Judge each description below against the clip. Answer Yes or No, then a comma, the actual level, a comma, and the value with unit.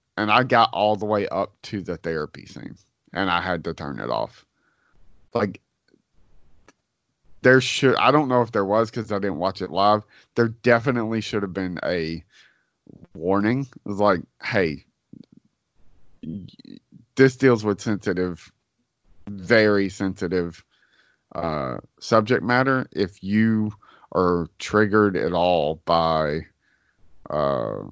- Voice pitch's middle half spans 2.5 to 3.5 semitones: No, average, 4.2 semitones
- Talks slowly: Yes, slow, 130 wpm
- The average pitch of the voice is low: Yes, low, 100 Hz